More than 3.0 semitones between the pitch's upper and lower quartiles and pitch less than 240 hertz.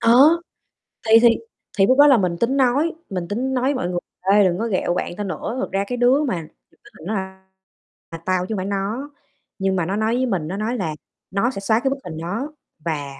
Yes: average, 5.2 semitones; high, 205 Hz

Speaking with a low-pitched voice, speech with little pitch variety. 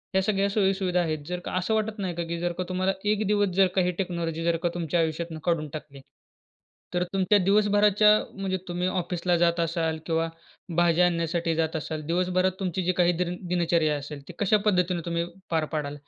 No: medium, 175 Hz; narrow, 2.3 semitones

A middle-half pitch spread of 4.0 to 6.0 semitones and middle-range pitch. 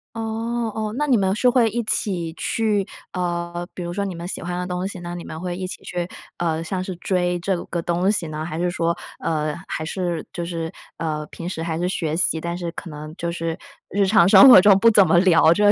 No: average, 2.8 semitones; medium, 175 Hz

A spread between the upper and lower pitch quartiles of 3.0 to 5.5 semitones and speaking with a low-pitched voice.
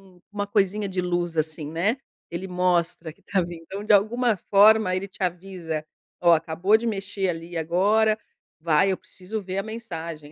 No: average, 3.4 semitones; medium, 185 Hz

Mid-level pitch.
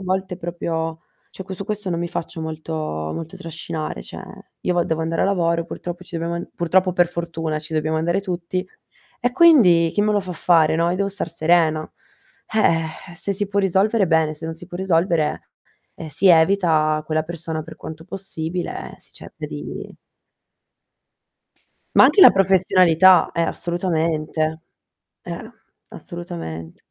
Yes: medium, 170 Hz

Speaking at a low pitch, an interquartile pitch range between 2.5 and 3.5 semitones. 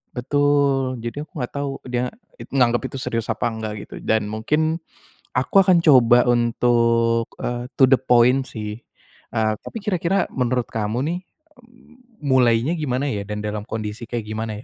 No: low, 125 Hz; average, 3.9 semitones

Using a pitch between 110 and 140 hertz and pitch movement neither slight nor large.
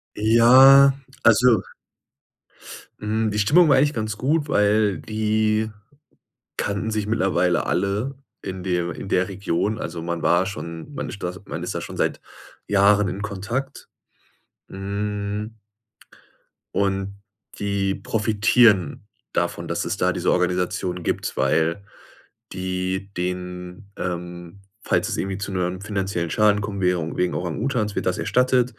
No: low, 100 Hz; average, 3.1 semitones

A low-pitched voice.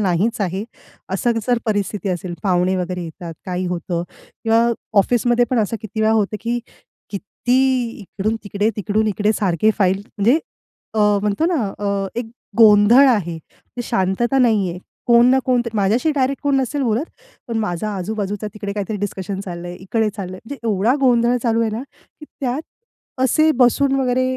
No: high, 215 Hz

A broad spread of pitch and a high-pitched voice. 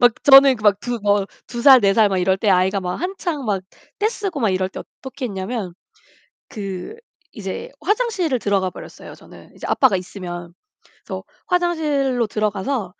Yes: wide, 6.3 semitones; high, 220 Hz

